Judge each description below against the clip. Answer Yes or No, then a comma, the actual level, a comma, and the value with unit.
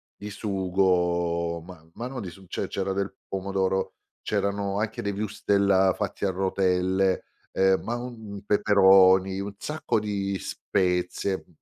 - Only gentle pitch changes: Yes, narrow, 1.4 semitones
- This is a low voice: Yes, very low, 95 Hz